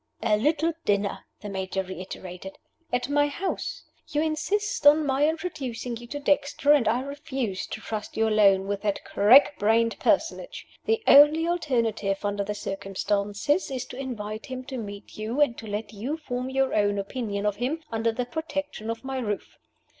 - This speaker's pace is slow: No, average, 175 wpm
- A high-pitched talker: Yes, high, 235 Hz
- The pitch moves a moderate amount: No, wide, 5.8 semitones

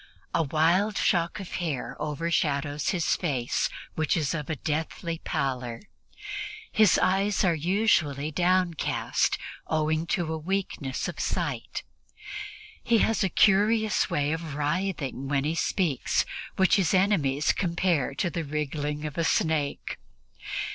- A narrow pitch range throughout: No, average, 4.0 semitones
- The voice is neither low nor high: Yes, medium, 160 Hz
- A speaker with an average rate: No, slow, 130 wpm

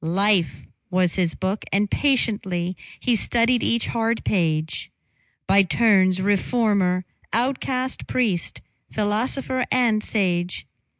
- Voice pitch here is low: No, high, 205 Hz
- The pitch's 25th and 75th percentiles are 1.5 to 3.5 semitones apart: No, average, 4.3 semitones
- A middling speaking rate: No, slow, 105 wpm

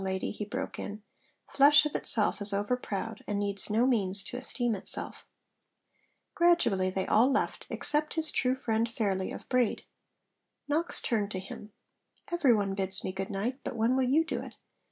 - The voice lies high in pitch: Yes, high, 220 Hz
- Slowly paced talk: No, average, 175 wpm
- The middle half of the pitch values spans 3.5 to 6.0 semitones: Yes, average, 4.8 semitones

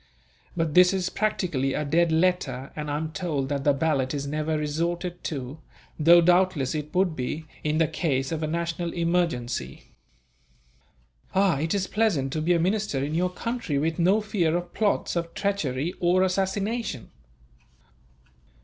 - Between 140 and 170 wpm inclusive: Yes, average, 160 wpm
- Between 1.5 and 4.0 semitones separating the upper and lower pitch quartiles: Yes, average, 3.6 semitones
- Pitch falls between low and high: Yes, medium, 165 Hz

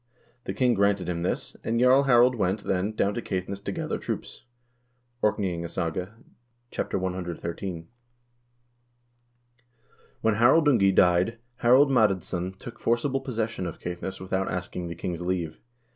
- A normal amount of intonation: Yes, average, 4.6 semitones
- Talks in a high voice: No, very low, 95 Hz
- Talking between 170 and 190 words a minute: No, slow, 135 wpm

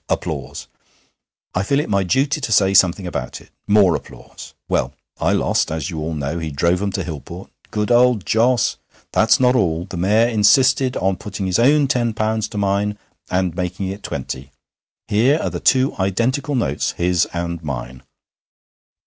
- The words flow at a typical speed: Yes, average, 175 wpm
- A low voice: Yes, low, 100 Hz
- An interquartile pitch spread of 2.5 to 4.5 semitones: No, wide, 5.4 semitones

